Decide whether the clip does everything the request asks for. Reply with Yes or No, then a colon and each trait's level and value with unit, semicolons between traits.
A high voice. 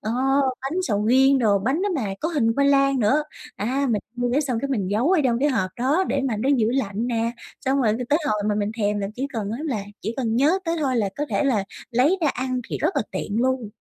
Yes: very high, 250 Hz